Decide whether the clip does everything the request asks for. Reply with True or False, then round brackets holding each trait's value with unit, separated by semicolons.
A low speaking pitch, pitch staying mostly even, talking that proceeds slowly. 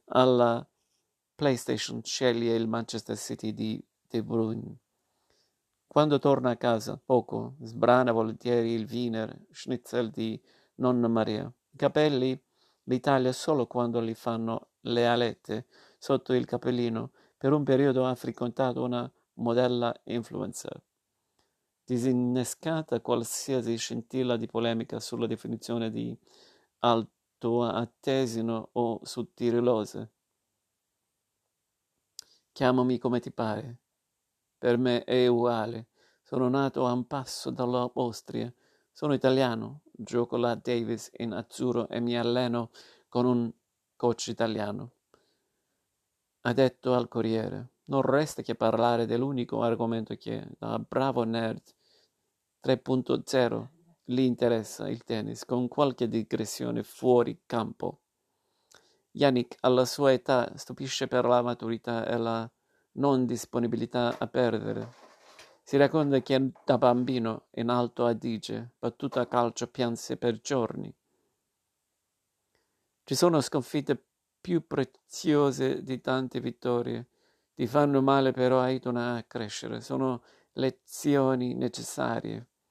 True (120 Hz; 1.9 semitones; 110 wpm)